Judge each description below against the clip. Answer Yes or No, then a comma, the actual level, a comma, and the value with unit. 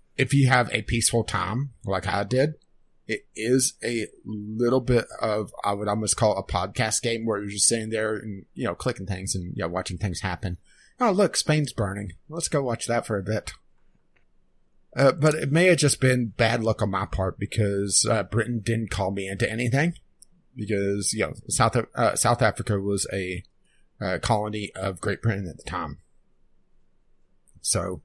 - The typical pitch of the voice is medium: No, low, 110 Hz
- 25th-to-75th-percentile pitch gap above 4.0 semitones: No, average, 3.4 semitones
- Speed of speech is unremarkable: Yes, average, 190 wpm